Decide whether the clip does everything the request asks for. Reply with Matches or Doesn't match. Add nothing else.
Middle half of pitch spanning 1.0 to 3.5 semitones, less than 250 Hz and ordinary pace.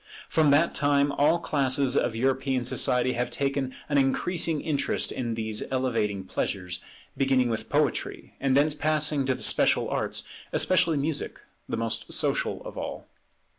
Matches